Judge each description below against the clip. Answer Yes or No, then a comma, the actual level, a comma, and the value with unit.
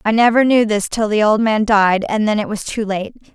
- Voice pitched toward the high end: Yes, high, 215 Hz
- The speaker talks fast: Yes, fast, 270 wpm